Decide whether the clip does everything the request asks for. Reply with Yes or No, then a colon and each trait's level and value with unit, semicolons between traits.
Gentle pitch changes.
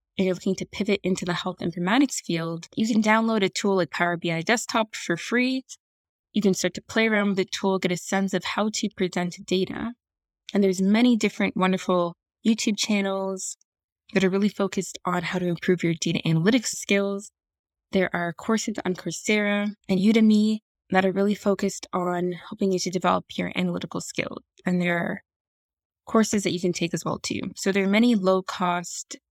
No: average, 3.0 semitones